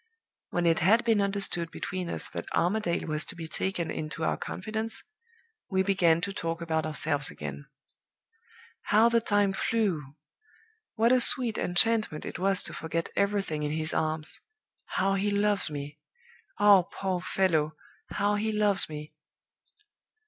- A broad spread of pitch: No, average, 4.4 semitones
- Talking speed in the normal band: Yes, average, 150 wpm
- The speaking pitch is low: No, medium, 185 Hz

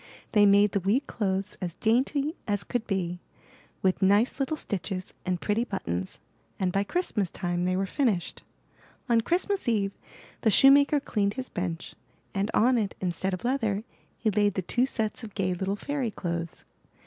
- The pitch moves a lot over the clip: No, average, 4.3 semitones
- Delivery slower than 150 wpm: No, average, 170 wpm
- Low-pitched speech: No, high, 205 Hz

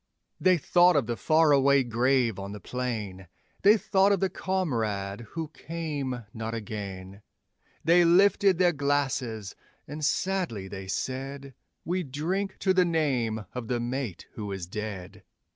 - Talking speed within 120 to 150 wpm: Yes, average, 145 wpm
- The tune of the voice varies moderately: No, wide, 7.5 semitones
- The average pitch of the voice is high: No, low, 135 Hz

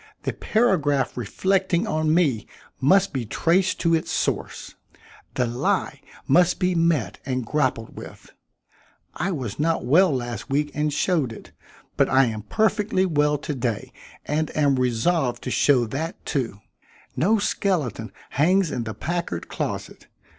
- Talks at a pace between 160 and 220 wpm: No, average, 145 wpm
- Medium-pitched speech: Yes, medium, 150 Hz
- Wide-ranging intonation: Yes, wide, 5.8 semitones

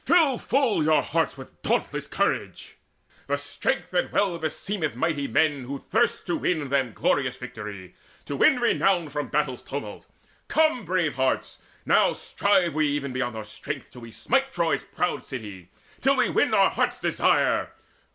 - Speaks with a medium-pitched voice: Yes, medium, 145 Hz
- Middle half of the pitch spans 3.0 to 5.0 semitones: No, wide, 5.6 semitones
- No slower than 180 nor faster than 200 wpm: No, average, 160 wpm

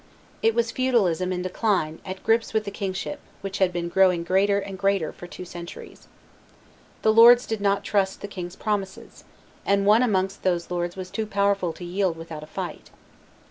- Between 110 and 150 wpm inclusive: No, average, 180 wpm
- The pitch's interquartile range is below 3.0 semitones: Yes, narrow, 2.5 semitones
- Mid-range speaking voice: No, high, 195 Hz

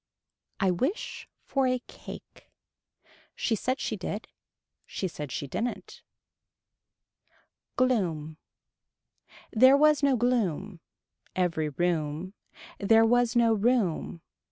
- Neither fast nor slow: No, slow, 100 wpm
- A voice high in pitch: Yes, high, 215 Hz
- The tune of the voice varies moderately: No, wide, 6.4 semitones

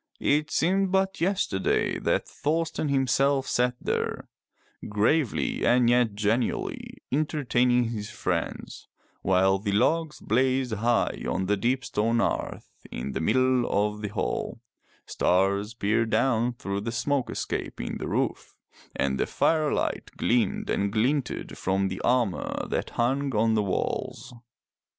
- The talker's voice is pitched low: Yes, low, 120 Hz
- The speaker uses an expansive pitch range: No, average, 4.6 semitones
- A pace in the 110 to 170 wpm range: Yes, slow, 135 wpm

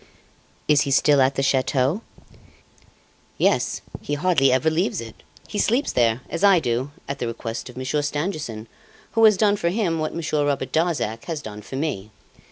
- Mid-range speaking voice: Yes, medium, 145 Hz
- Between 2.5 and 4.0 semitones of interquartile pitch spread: No, average, 4.7 semitones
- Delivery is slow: No, average, 175 wpm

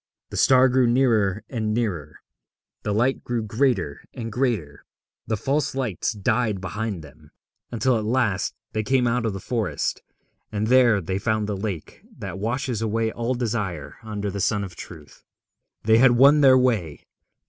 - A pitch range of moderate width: Yes, average, 4.0 semitones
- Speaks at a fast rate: No, average, 165 wpm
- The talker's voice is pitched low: Yes, low, 110 Hz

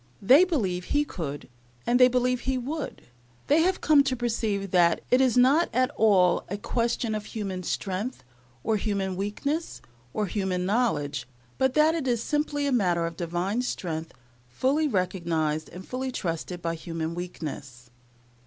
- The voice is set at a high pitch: Yes, high, 210 Hz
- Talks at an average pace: Yes, average, 160 wpm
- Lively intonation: Yes, wide, 6.5 semitones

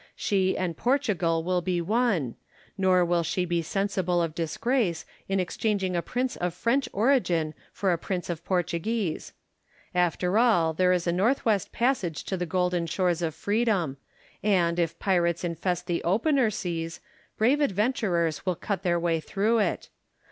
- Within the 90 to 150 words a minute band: No, average, 160 wpm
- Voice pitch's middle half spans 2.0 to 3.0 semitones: No, average, 3.7 semitones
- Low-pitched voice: No, medium, 180 Hz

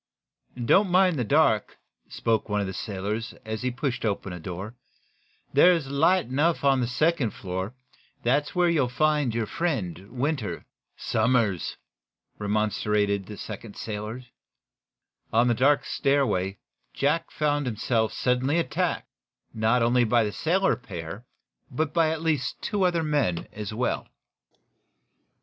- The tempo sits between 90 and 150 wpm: Yes, average, 140 wpm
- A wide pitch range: Yes, wide, 6.0 semitones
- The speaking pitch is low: Yes, low, 125 Hz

